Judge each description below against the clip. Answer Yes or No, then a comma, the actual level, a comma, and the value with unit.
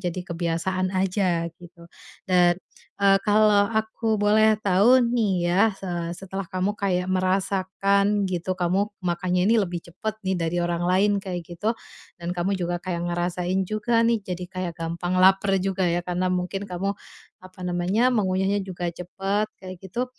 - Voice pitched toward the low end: No, medium, 185 Hz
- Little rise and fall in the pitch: Yes, narrow, 2.1 semitones